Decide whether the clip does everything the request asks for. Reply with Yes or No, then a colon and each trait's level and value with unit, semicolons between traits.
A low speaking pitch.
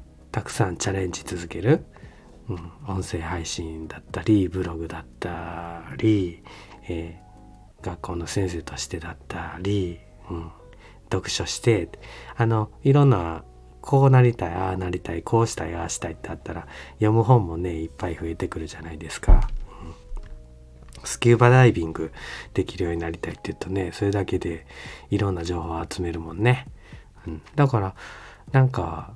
Yes: very low, 90 Hz